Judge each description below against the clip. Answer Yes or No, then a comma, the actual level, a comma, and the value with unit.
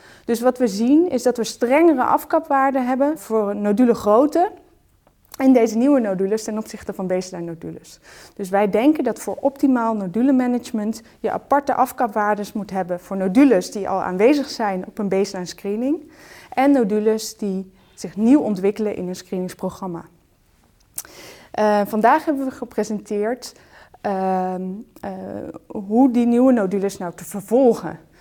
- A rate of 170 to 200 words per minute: No, average, 145 wpm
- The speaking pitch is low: No, high, 220 Hz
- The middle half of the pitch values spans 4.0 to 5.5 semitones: Yes, average, 4.7 semitones